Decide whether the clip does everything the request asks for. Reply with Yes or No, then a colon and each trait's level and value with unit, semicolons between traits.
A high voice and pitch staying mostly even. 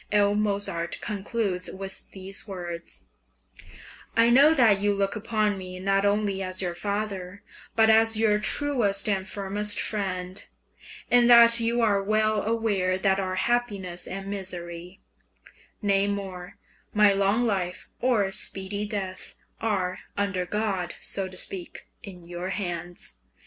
Yes: high, 200 Hz; narrow, 2.3 semitones